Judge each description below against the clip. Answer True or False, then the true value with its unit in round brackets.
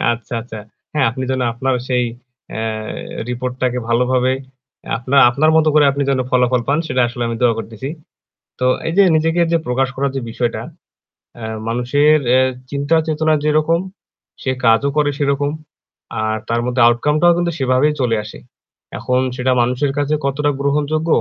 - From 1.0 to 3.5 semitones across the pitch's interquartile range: True (3.2 semitones)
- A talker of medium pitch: False (130 Hz)